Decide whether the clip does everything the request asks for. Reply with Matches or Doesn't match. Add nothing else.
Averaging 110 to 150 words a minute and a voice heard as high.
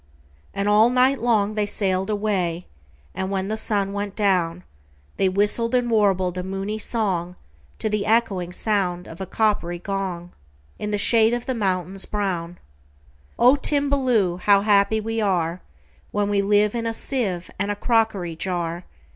Matches